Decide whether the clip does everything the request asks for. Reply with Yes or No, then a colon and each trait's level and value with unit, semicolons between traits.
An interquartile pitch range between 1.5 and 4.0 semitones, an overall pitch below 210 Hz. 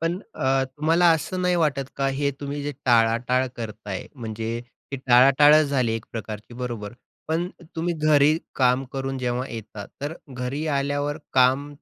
Yes: average, 3.4 semitones; low, 135 Hz